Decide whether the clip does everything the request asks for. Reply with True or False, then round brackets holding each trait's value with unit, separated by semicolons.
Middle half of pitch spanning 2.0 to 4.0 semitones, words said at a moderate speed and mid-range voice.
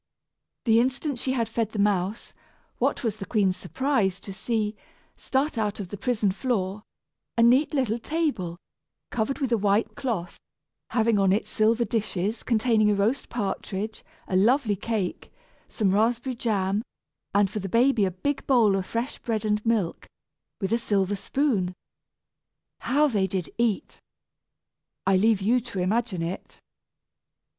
False (3.5 semitones; 150 wpm; 215 Hz)